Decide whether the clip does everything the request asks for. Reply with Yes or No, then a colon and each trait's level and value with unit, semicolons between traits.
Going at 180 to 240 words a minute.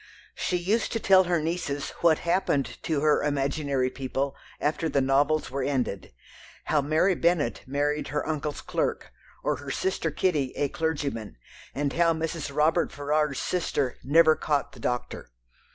No: average, 150 wpm